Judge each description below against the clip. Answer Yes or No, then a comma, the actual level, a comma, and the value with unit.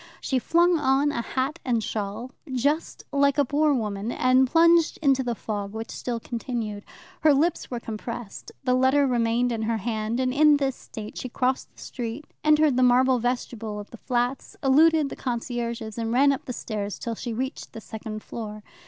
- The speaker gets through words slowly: No, average, 190 wpm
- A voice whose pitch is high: Yes, high, 245 Hz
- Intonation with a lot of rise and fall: No, average, 3.4 semitones